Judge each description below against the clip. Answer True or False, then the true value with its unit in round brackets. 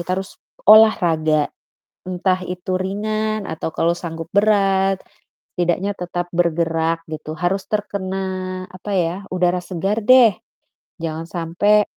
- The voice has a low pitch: False (185 Hz)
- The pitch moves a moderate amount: True (3.0 semitones)